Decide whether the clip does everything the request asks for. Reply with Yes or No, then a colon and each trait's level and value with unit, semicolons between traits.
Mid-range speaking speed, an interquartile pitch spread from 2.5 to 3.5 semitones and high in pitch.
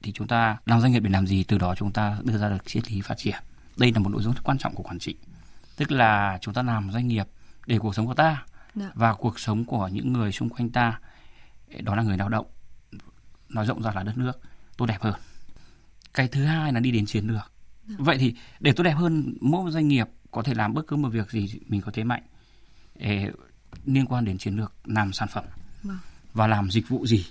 No: average, 240 wpm; average, 3.2 semitones; low, 110 Hz